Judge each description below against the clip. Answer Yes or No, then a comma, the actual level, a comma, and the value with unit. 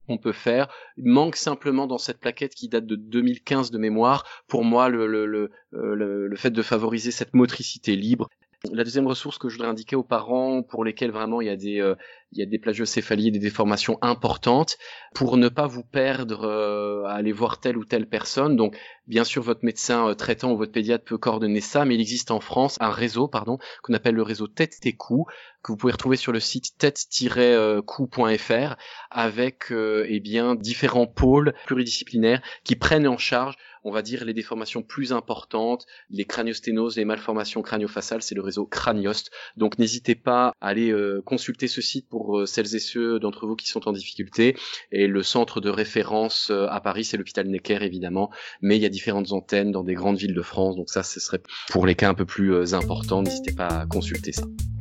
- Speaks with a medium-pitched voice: No, low, 115 Hz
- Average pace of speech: Yes, average, 205 wpm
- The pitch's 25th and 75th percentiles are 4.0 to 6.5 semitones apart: No, average, 2.8 semitones